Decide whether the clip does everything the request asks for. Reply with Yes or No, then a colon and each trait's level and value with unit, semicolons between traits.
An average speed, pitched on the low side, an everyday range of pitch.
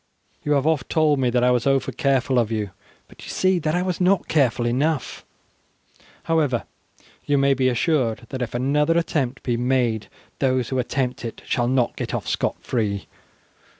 Yes: average, 185 wpm; low, 130 Hz; average, 3.5 semitones